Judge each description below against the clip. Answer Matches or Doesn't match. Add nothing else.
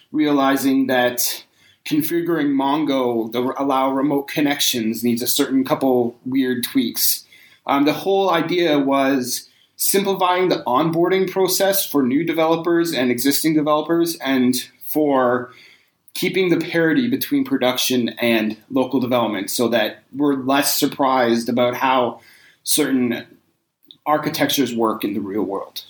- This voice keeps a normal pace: Doesn't match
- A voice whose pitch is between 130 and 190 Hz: Matches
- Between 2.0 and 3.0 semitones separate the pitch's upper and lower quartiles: Doesn't match